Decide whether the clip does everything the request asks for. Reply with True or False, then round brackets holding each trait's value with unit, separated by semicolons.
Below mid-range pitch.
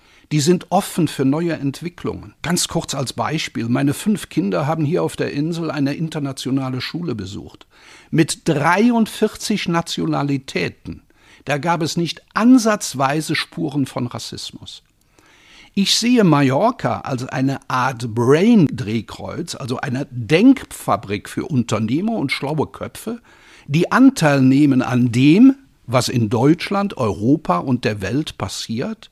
False (145 Hz)